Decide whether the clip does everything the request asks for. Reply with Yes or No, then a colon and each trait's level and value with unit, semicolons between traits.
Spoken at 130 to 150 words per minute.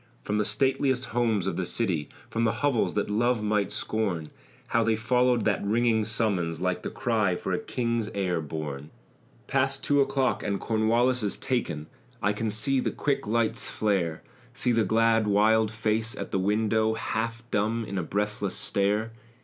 No: average, 170 wpm